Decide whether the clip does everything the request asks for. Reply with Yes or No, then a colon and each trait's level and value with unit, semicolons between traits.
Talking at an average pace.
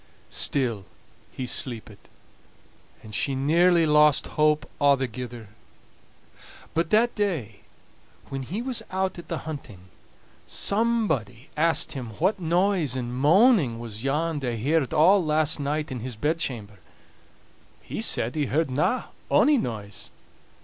No: slow, 120 wpm